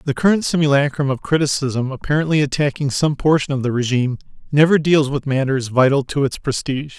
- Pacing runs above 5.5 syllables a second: Yes, 6.0 syllables/s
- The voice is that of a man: Yes, male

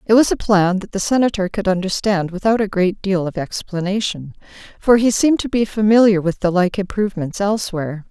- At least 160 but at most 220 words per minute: Yes, average, 190 wpm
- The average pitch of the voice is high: Yes, high, 195 Hz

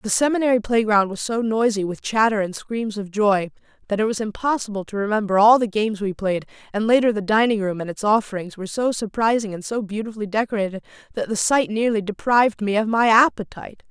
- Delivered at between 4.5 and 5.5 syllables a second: No, 6.1 syllables/s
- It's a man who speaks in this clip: No, female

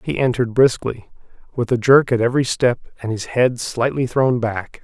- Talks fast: No, average, 185 wpm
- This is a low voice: Yes, low, 125 Hz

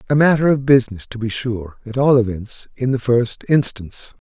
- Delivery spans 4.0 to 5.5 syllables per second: Yes, 5.3 syllables/s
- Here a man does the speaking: Yes, male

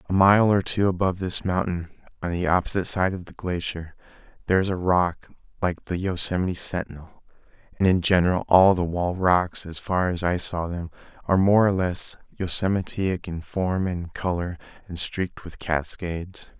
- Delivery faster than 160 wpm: Yes, average, 175 wpm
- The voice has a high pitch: No, very low, 90 Hz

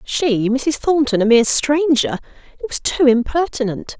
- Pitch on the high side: Yes, very high, 250 Hz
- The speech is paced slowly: Yes, slow, 120 wpm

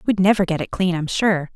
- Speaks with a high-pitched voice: No, medium, 180 Hz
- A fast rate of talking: Yes, fast, 270 wpm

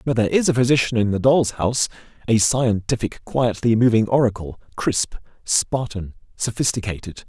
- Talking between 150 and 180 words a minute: No, average, 140 wpm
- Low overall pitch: Yes, low, 115 Hz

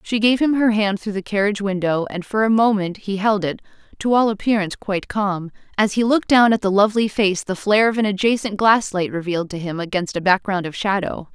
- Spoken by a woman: Yes, female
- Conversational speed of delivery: No, fast, 225 wpm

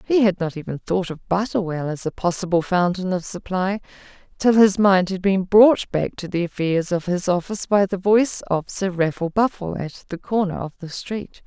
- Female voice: Yes, female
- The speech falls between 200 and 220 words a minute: Yes, fast, 205 wpm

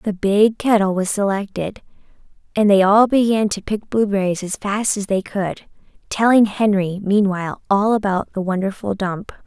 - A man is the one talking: No, female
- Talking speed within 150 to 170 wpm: Yes, average, 160 wpm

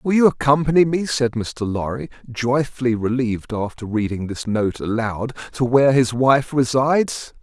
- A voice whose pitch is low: Yes, low, 125 Hz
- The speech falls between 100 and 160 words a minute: Yes, average, 155 wpm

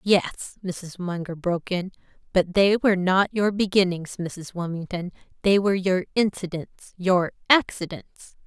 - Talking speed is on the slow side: Yes, slow, 130 wpm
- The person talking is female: Yes, female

